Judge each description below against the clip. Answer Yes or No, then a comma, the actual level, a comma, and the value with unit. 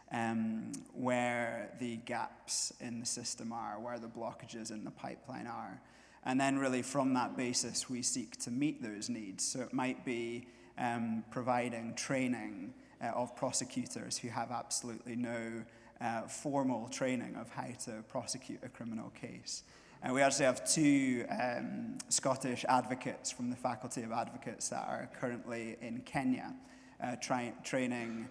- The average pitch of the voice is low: Yes, low, 125 Hz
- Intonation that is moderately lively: No, narrow, 2.2 semitones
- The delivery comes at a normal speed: Yes, average, 155 wpm